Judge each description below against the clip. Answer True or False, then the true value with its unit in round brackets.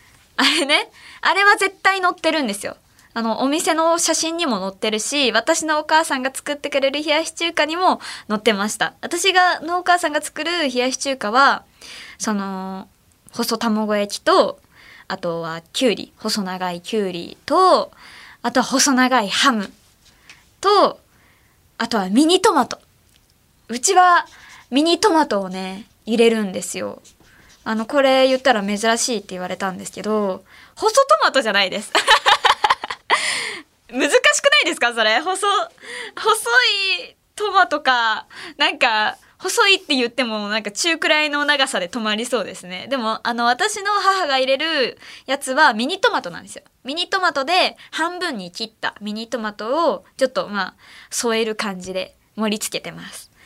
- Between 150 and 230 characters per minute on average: False (300 characters per minute)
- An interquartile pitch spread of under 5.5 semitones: False (7.3 semitones)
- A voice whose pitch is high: True (270 Hz)